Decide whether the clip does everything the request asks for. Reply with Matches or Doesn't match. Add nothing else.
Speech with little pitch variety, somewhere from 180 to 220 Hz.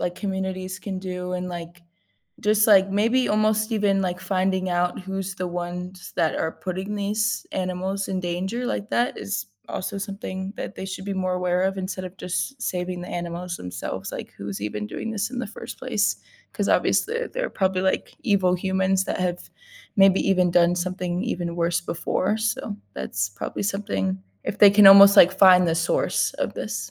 Matches